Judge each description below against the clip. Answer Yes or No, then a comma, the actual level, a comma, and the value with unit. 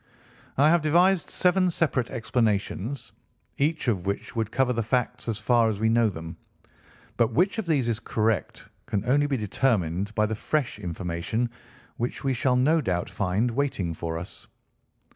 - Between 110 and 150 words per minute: No, average, 165 wpm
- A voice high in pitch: No, low, 115 Hz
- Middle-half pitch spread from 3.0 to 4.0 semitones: No, average, 5.2 semitones